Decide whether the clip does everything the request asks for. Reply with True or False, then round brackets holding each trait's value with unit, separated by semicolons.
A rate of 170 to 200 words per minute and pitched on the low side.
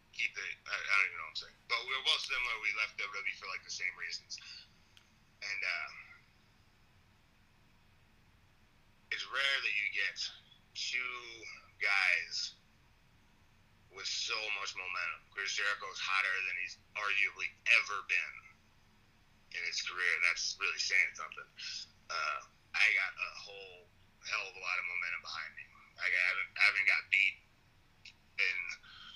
False (140 wpm; 120 Hz)